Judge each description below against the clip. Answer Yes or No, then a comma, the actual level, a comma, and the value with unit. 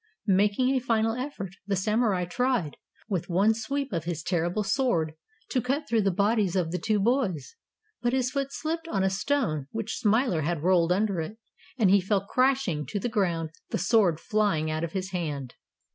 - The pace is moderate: Yes, average, 190 wpm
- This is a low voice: No, high, 200 Hz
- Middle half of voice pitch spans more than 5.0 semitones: Yes, wide, 5.6 semitones